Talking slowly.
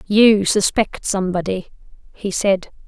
Yes: slow, 105 wpm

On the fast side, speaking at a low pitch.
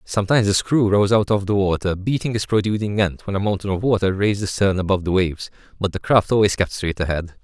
Yes: fast, 240 wpm; low, 100 Hz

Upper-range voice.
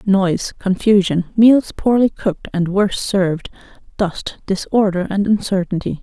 Yes: high, 195 Hz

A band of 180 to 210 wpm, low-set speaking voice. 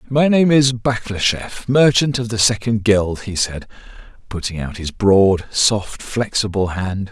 No: average, 150 wpm; low, 110 Hz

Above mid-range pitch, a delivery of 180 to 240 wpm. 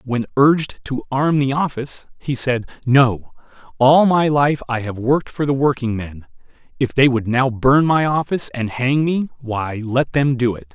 No: low, 130 Hz; average, 185 wpm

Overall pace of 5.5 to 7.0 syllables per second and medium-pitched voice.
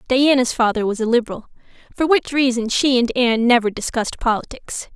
No: 5.9 syllables/s; high, 240 Hz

